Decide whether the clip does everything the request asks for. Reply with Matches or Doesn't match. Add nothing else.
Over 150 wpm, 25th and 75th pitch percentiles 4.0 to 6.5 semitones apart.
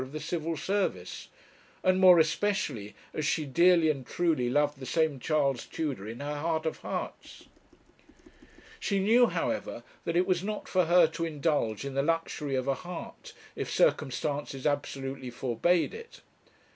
Matches